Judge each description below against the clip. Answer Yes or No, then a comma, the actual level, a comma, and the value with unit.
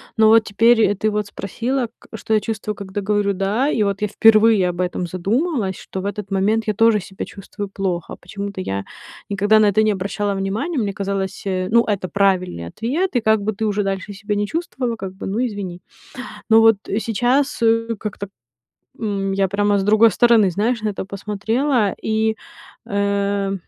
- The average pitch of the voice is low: No, high, 205 Hz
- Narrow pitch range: Yes, narrow, 2.3 semitones